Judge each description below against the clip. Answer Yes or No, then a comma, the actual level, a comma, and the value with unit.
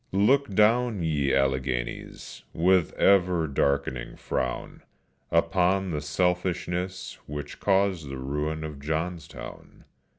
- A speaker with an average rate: No, slow, 105 wpm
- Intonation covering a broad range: No, average, 4.8 semitones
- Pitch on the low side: Yes, very low, 85 Hz